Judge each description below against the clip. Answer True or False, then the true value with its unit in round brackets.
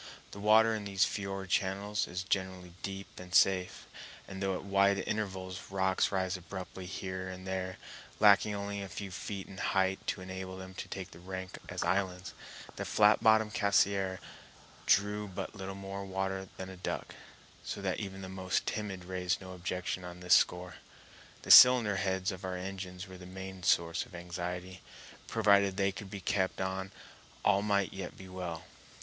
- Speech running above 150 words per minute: True (175 wpm)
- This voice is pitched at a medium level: False (95 Hz)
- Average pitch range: False (1.1 semitones)